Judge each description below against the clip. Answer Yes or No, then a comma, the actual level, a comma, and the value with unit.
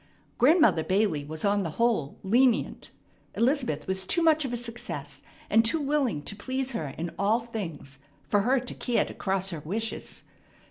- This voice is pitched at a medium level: No, high, 220 Hz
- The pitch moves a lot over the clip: Yes, wide, 6.1 semitones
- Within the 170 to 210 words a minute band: Yes, average, 175 wpm